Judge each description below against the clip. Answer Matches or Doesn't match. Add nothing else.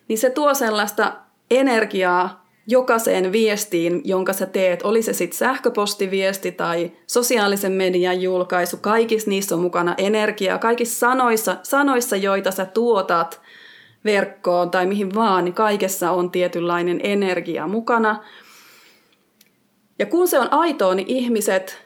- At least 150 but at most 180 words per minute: Doesn't match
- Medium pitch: Doesn't match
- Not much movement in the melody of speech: Doesn't match